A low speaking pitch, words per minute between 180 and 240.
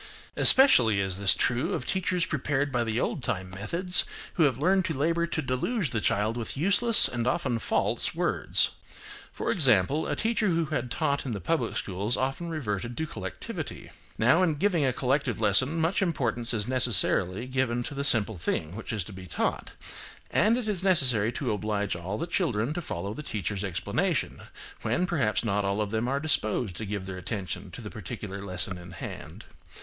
Yes: low, 120 Hz; average, 190 wpm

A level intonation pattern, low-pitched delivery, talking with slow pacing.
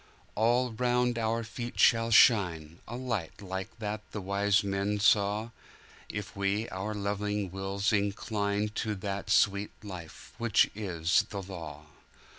Yes: narrow, 2.2 semitones; low, 105 Hz; slow, 125 wpm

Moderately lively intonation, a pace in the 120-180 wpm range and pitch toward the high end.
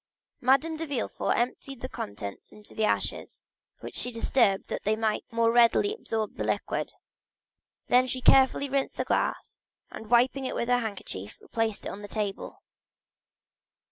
Yes: average, 3.5 semitones; average, 165 wpm; high, 235 Hz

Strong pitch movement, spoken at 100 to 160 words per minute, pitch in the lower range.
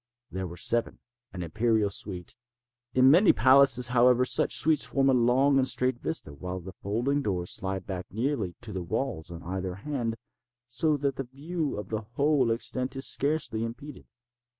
No: wide, 5.7 semitones; average, 170 wpm; low, 120 Hz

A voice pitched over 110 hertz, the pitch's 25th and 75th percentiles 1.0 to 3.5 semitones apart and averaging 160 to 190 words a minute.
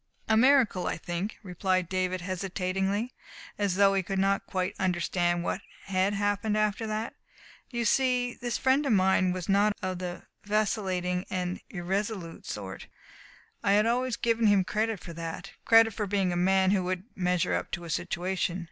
Yes: high, 190 Hz; average, 2.8 semitones; average, 170 wpm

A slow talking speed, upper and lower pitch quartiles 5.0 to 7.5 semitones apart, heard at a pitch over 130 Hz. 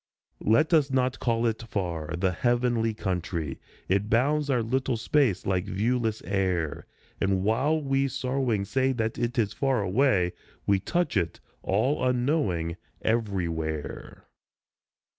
No: slow, 130 wpm; wide, 5.4 semitones; low, 115 Hz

